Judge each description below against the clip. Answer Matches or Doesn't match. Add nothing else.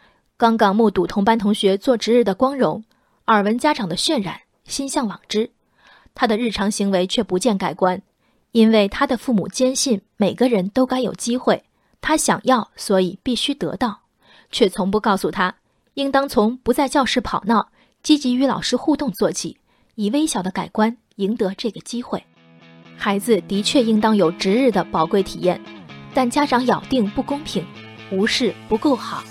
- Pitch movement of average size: Matches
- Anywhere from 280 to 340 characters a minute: Doesn't match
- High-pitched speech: Matches